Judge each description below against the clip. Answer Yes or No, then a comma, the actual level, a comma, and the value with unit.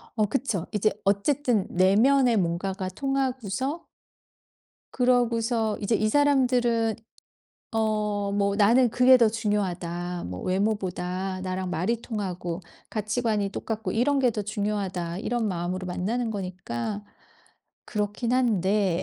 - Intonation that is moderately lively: Yes, average, 4.2 semitones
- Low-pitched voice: No, high, 210 Hz